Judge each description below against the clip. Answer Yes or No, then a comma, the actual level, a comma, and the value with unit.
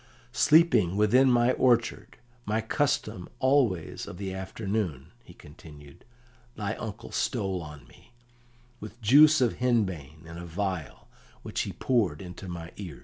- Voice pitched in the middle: No, low, 100 Hz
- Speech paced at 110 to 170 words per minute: Yes, average, 140 wpm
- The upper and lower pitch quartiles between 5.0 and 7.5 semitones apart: Yes, wide, 5.6 semitones